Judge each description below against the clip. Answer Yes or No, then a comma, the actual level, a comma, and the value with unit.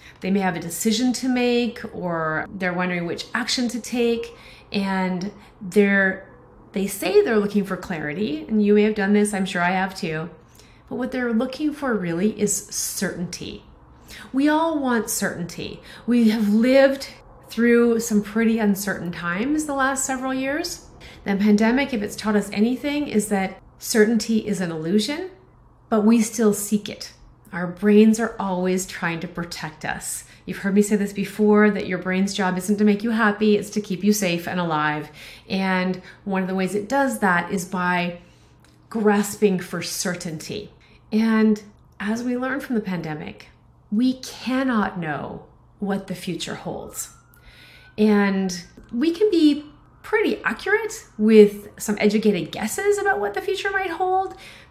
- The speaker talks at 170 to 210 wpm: No, average, 160 wpm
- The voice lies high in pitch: Yes, high, 210 Hz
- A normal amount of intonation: Yes, average, 4.1 semitones